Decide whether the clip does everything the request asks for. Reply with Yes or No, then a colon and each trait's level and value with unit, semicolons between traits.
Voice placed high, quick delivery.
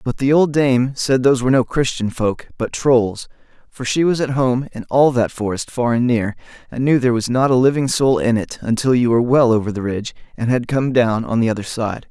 No: low, 125 Hz; fast, 245 wpm